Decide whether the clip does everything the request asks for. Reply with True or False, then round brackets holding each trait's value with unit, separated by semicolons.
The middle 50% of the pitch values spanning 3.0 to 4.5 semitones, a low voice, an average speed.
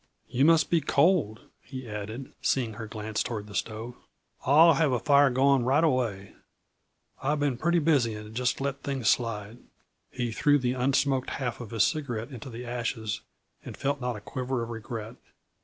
True (3.7 semitones; 125 Hz; 180 wpm)